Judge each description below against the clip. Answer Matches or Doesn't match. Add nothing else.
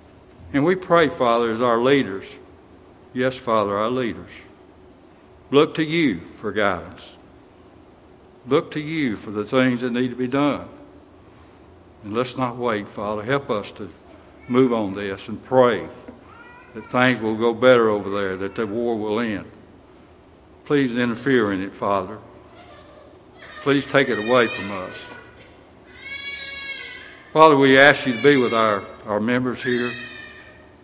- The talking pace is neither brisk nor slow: Matches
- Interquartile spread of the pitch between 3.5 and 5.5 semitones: Matches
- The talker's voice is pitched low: Matches